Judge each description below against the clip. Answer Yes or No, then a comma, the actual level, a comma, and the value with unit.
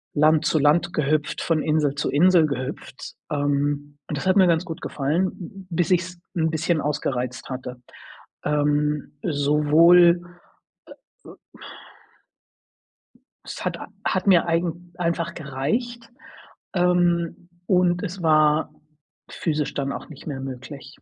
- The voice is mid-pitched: Yes, medium, 155 Hz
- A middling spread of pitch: Yes, average, 3.2 semitones